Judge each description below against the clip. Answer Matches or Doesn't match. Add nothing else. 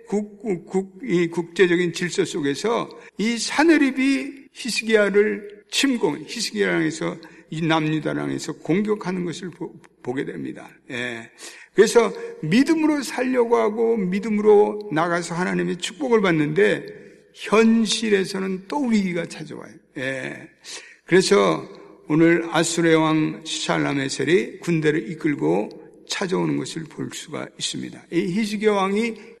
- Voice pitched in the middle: Doesn't match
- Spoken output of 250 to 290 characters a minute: Matches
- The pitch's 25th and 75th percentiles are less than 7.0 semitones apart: Matches